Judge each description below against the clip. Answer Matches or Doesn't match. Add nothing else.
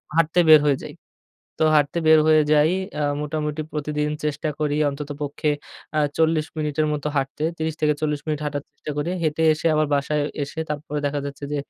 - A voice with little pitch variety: Matches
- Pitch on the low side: Doesn't match